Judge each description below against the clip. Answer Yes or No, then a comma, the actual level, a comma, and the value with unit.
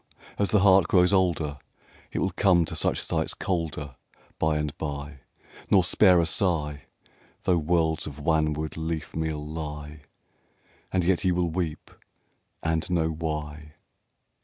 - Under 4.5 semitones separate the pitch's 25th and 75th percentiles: Yes, average, 2.7 semitones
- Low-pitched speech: Yes, very low, 80 Hz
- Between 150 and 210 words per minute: No, slow, 135 wpm